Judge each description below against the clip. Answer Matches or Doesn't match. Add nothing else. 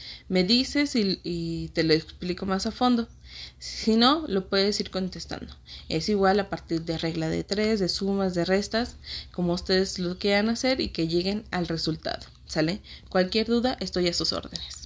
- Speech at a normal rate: Matches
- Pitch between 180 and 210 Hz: Matches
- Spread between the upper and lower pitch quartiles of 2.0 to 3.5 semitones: Doesn't match